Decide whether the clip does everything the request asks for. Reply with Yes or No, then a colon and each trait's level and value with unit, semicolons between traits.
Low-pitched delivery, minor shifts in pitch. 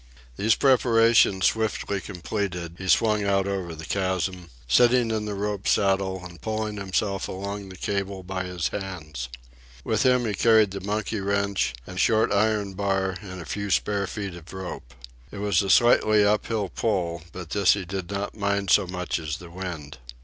Yes: low, 100 Hz; narrow, 2.3 semitones